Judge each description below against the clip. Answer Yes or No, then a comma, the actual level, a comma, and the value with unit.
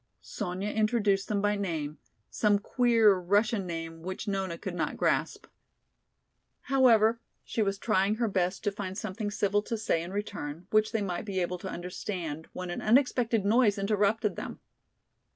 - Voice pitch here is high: Yes, high, 200 Hz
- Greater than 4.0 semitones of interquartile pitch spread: No, average, 2.9 semitones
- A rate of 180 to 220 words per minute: No, average, 160 wpm